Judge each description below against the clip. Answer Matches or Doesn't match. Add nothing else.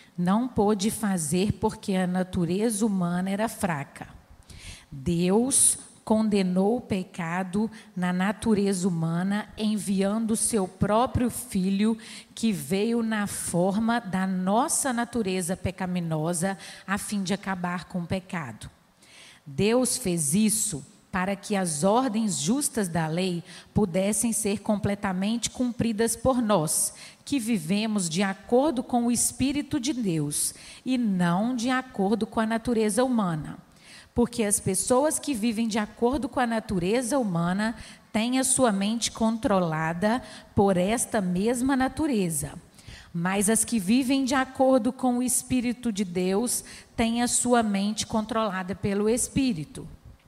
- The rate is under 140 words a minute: Matches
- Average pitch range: Matches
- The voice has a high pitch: Matches